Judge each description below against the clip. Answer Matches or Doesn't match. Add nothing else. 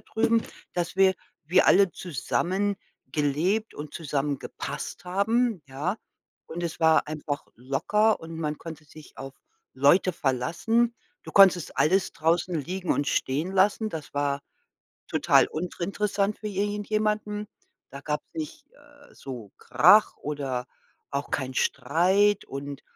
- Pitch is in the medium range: Matches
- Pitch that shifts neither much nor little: Doesn't match